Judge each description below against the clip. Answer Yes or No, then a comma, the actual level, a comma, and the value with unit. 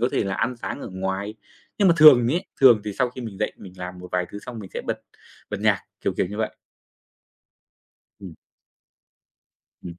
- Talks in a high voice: No, low, 105 Hz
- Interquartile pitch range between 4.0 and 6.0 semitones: Yes, average, 4.6 semitones